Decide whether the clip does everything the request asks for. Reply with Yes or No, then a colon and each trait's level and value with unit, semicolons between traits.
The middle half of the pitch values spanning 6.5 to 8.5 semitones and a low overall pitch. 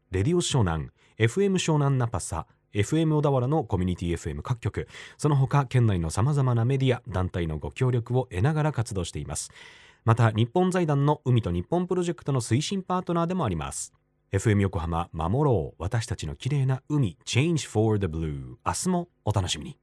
Yes: wide, 8.0 semitones; low, 120 Hz